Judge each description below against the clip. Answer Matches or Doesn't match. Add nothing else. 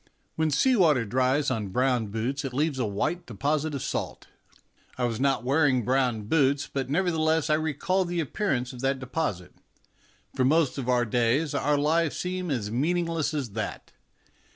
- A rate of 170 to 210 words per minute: Matches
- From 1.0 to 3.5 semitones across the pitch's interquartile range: Doesn't match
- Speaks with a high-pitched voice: Doesn't match